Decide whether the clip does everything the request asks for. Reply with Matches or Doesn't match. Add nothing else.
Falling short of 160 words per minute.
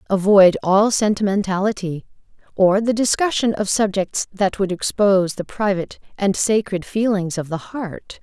Matches